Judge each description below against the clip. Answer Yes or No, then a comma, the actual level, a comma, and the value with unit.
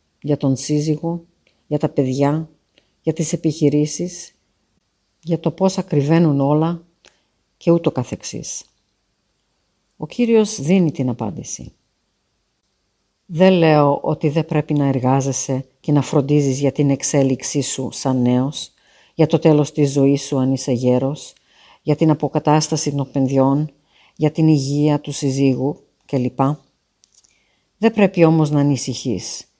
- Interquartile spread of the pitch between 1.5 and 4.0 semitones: Yes, average, 2.8 semitones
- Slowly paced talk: No, average, 130 wpm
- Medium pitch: Yes, medium, 145 Hz